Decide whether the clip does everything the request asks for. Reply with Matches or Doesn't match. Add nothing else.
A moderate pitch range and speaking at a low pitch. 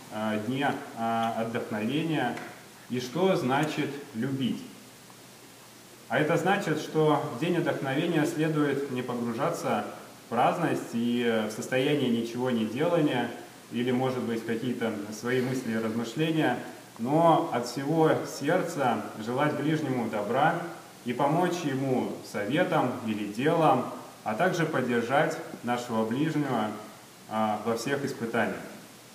Matches